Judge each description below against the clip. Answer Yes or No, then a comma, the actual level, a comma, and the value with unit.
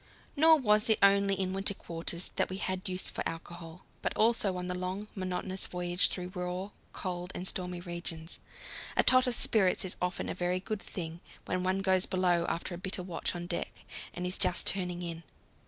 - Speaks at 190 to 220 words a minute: Yes, average, 195 wpm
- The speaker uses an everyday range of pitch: No, narrow, 1.6 semitones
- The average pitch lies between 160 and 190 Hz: Yes, medium, 185 Hz